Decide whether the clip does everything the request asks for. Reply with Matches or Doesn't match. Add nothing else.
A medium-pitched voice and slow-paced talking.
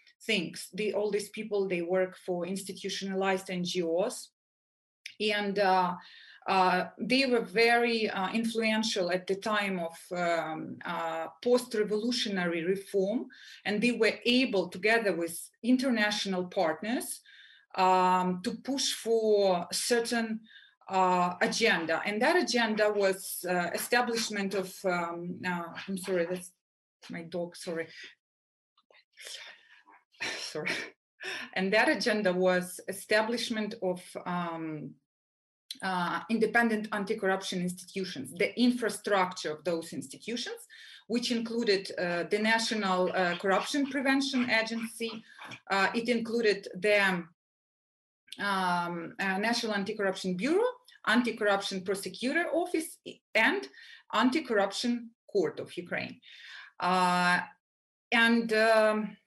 Doesn't match